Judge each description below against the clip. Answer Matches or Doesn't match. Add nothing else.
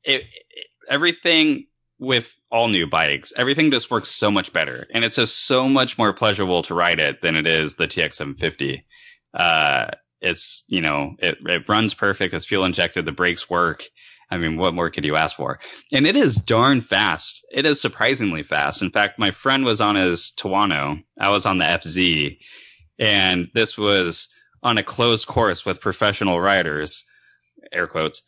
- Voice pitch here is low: Matches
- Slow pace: Doesn't match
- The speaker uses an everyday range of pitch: Doesn't match